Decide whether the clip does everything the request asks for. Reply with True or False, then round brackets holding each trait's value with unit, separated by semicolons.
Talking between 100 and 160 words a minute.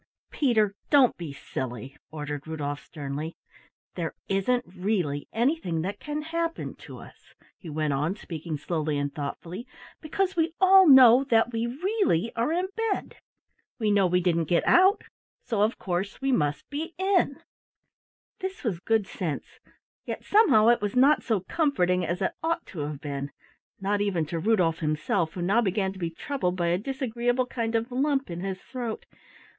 False (170 wpm)